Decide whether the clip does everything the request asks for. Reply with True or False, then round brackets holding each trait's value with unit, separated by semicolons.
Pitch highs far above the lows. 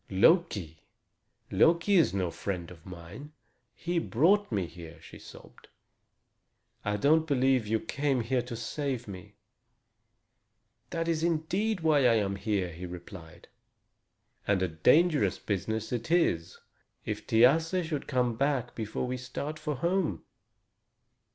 True (8.4 semitones)